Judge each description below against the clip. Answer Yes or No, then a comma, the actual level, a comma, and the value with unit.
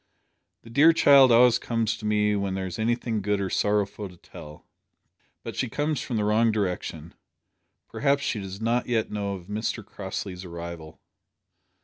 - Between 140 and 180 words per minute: Yes, average, 165 wpm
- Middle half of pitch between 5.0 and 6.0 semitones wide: No, average, 3.4 semitones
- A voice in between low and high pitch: No, low, 105 Hz